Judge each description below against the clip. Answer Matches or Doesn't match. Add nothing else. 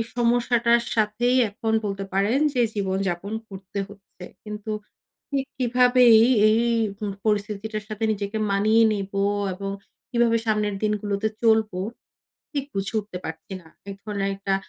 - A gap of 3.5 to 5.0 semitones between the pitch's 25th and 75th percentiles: Doesn't match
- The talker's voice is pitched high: Matches